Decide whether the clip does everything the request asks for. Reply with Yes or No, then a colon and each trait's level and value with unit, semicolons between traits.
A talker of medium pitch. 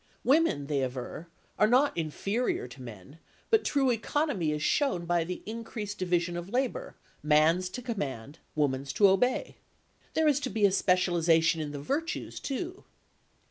Yes: medium, 180 Hz